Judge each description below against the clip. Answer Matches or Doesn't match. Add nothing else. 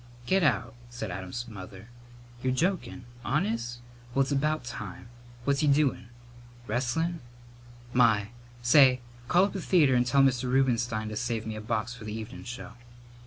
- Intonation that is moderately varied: Matches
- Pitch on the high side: Doesn't match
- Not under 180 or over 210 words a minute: Doesn't match